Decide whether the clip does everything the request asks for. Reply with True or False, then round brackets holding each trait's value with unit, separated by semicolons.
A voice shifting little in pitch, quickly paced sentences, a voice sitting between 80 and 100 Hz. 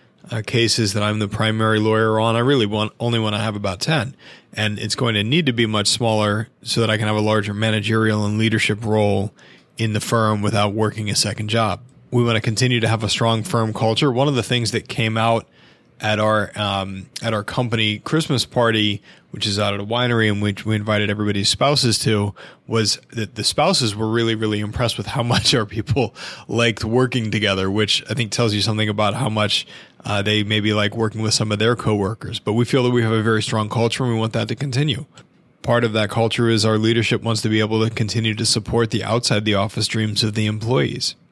False (1.7 semitones; 230 wpm; 110 Hz)